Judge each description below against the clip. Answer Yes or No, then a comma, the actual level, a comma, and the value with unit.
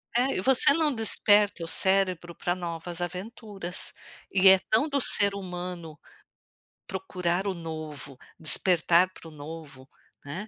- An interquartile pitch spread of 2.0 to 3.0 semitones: No, average, 3.4 semitones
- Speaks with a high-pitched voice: No, medium, 180 Hz